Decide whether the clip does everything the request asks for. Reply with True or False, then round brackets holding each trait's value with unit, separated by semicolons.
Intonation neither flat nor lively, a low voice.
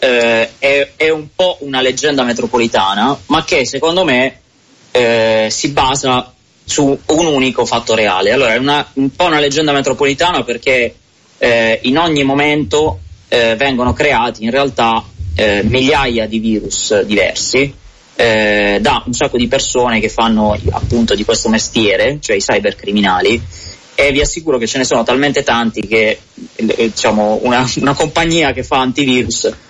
True (4.1 semitones; 125 Hz)